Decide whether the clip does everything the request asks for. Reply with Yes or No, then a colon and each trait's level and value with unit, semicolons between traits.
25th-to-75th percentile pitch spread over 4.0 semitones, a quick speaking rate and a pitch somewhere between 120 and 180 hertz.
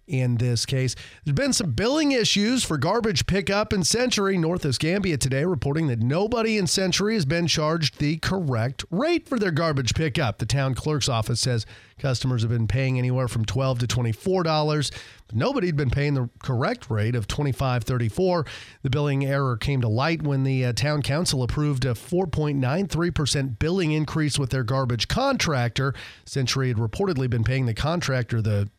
No: average, 5.1 semitones; average, 185 wpm; medium, 140 Hz